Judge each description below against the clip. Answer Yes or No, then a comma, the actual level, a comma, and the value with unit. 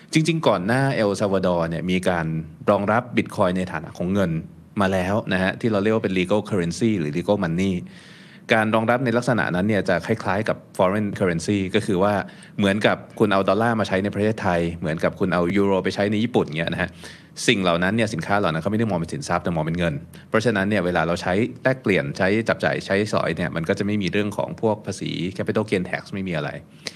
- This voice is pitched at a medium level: No, low, 100 Hz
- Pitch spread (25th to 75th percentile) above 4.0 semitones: No, average, 3.5 semitones